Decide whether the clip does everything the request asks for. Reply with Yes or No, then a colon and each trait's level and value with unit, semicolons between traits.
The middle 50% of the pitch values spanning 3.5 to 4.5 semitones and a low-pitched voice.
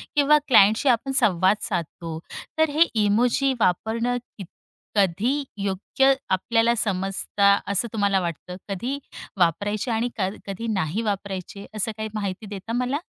No: average, 3.8 semitones; high, 210 Hz